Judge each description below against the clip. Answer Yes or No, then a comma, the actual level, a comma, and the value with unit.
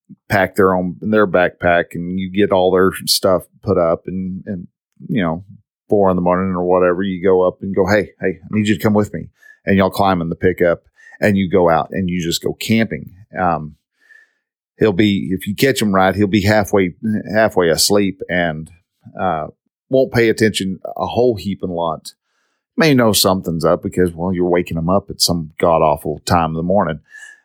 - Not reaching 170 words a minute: No, average, 200 wpm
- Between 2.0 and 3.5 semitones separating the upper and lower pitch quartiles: Yes, average, 3.1 semitones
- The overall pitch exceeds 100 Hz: No, very low, 95 Hz